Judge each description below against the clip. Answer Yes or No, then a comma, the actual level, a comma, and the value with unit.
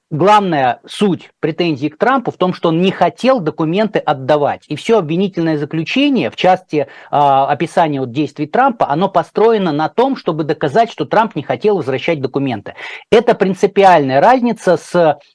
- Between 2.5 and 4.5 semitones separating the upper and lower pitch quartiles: No, wide, 5.5 semitones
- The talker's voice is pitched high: No, medium, 170 Hz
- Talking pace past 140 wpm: Yes, average, 155 wpm